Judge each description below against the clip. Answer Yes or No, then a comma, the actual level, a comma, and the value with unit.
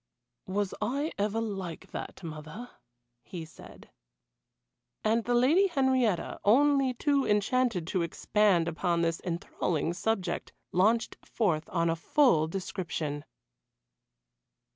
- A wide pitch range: Yes, wide, 6.4 semitones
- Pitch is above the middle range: Yes, high, 200 Hz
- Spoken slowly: Yes, slow, 110 wpm